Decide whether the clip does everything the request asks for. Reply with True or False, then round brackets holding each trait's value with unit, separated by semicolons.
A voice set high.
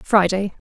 True (195 Hz)